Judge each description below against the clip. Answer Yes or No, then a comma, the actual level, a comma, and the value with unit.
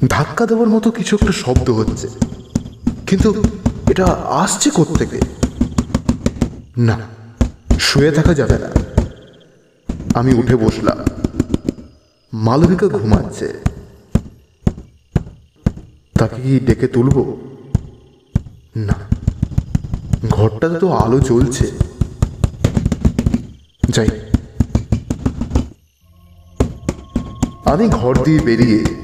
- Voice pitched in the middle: No, low, 115 Hz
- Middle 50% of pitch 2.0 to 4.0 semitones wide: Yes, average, 3.2 semitones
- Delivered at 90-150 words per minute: No, average, 75 wpm